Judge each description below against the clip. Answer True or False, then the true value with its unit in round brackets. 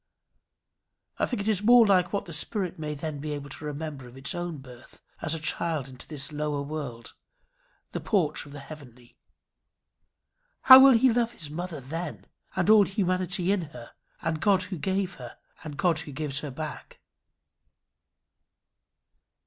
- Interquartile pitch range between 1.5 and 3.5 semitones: False (4.6 semitones)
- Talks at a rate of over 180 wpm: False (165 wpm)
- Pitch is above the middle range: False (155 Hz)